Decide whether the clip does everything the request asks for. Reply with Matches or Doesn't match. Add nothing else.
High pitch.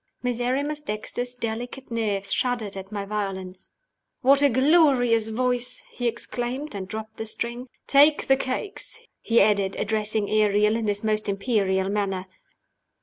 Matches